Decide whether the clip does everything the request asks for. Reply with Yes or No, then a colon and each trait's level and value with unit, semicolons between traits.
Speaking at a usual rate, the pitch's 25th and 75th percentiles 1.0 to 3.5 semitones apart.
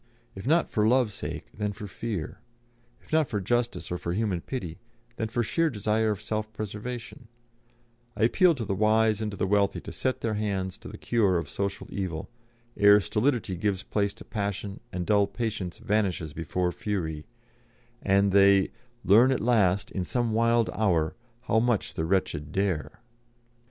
Yes: average, 170 wpm; average, 3.0 semitones